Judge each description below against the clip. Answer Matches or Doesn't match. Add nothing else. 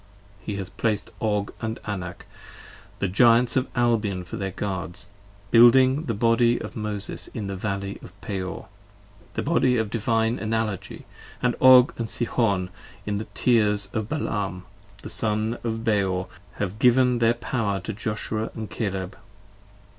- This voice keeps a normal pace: Matches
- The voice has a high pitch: Doesn't match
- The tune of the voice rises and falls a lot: Doesn't match